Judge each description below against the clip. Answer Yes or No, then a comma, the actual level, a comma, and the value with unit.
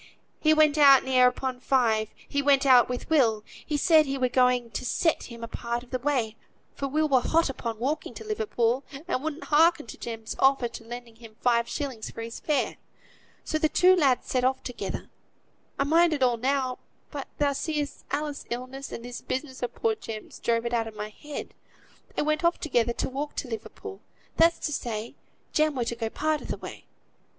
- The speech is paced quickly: Yes, fast, 210 wpm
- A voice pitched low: No, very high, 260 Hz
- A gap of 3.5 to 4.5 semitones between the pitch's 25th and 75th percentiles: Yes, average, 4.0 semitones